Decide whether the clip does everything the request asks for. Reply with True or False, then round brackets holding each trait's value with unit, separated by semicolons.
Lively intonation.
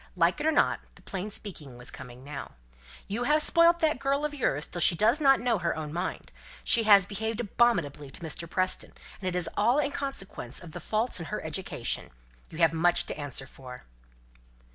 True (7.3 semitones)